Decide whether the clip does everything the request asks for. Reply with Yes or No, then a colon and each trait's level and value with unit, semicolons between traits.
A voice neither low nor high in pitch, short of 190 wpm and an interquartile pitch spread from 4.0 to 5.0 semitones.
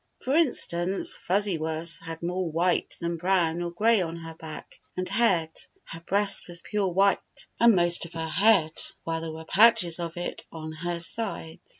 No: medium, 175 Hz; average, 180 wpm; average, 3.1 semitones